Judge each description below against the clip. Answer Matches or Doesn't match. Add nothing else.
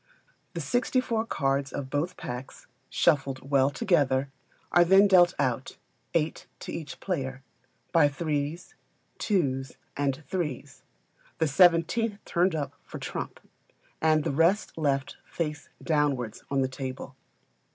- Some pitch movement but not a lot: Matches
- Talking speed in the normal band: Doesn't match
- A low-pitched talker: Doesn't match